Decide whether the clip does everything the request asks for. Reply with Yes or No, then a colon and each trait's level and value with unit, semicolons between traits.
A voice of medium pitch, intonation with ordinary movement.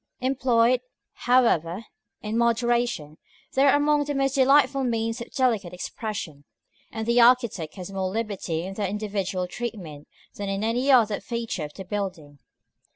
No: high, 225 Hz; average, 4.5 semitones